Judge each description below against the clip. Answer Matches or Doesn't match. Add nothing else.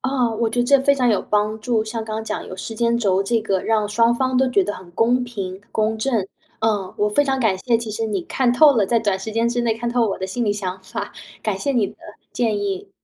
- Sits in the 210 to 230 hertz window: Matches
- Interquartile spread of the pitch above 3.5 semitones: Doesn't match